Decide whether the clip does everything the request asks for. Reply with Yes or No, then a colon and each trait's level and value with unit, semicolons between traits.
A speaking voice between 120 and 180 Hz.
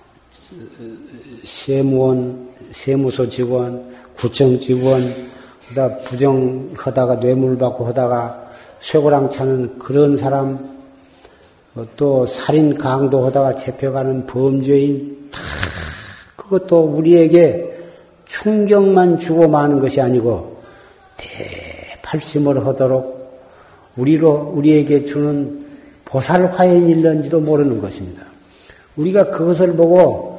Yes: low, 135 Hz